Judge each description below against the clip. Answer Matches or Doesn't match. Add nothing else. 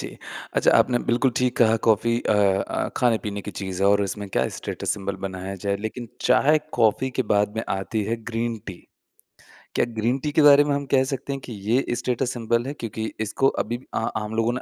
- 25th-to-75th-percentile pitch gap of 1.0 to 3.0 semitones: Doesn't match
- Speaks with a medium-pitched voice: Doesn't match